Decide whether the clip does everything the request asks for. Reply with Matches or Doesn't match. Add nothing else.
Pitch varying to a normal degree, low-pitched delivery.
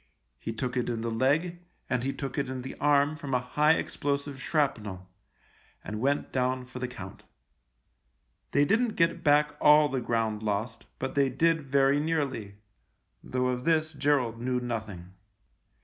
Matches